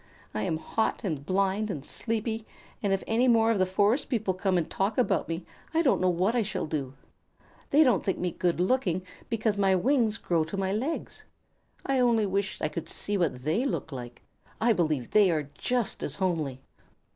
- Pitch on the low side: No, high, 195 Hz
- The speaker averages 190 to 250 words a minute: Yes, average, 200 wpm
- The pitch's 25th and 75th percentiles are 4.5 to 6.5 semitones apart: Yes, average, 5.1 semitones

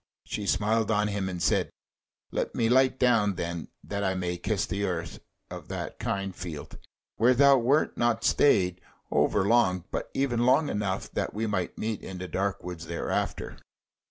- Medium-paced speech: Yes, average, 175 wpm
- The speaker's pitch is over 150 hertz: No, low, 100 Hz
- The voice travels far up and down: No, average, 4.2 semitones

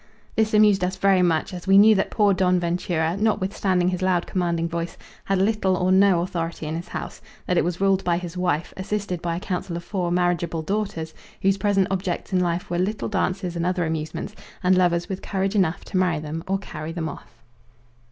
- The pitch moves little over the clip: Yes, narrow, 2.2 semitones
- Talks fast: Yes, fast, 210 wpm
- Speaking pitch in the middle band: Yes, medium, 180 Hz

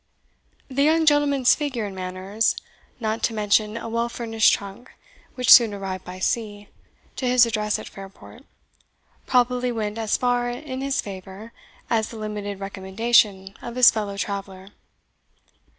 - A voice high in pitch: Yes, high, 220 Hz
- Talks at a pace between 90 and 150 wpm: Yes, average, 145 wpm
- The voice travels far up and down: No, average, 3.5 semitones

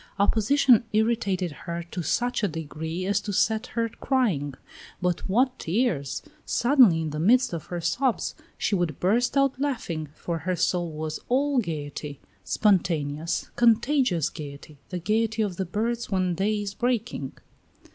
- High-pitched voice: Yes, high, 195 Hz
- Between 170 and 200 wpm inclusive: No, average, 150 wpm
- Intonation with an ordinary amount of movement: No, wide, 6.4 semitones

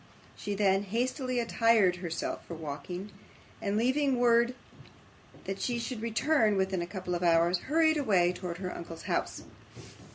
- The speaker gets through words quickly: No, average, 150 wpm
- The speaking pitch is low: No, high, 205 Hz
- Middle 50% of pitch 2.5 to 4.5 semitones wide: No, average, 5.2 semitones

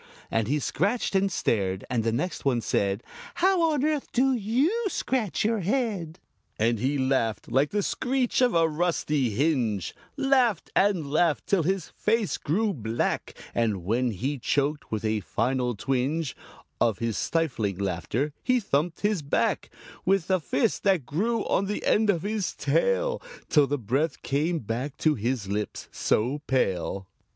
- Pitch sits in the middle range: Yes, medium, 150 Hz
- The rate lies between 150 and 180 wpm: Yes, average, 160 wpm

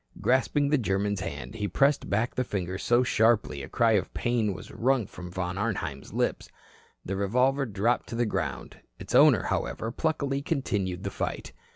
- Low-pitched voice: Yes, low, 110 Hz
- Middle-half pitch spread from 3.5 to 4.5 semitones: No, average, 5.0 semitones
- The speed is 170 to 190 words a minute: Yes, average, 175 wpm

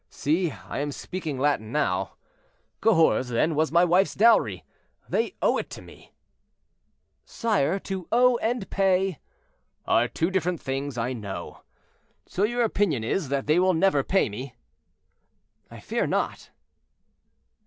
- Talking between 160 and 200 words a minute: No, average, 140 wpm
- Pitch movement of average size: No, wide, 6.1 semitones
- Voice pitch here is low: No, medium, 165 Hz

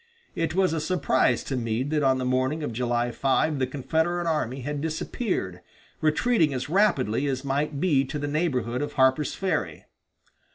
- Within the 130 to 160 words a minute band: No, average, 170 wpm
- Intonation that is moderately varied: Yes, average, 3.7 semitones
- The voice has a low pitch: No, medium, 145 Hz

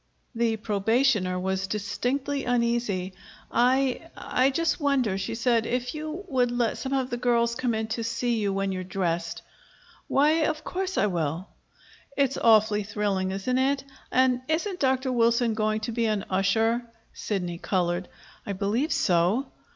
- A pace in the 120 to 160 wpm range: Yes, average, 155 wpm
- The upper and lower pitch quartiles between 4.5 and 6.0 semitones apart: Yes, average, 4.8 semitones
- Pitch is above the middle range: Yes, high, 230 Hz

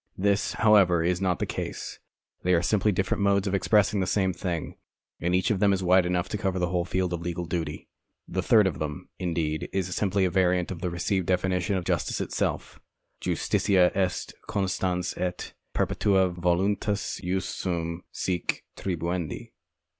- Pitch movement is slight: Yes, narrow, 1.8 semitones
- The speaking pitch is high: No, very low, 90 Hz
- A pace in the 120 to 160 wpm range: No, average, 170 wpm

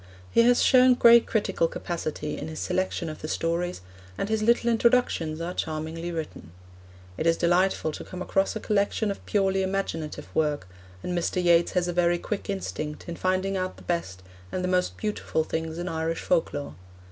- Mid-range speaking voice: Yes, medium, 175 Hz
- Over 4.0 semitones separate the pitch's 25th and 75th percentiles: No, average, 3.3 semitones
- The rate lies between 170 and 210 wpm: Yes, average, 180 wpm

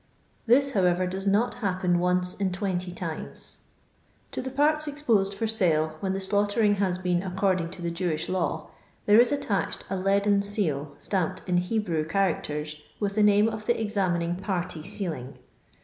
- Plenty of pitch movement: No, average, 2.8 semitones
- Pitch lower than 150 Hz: No, high, 190 Hz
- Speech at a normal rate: Yes, average, 165 wpm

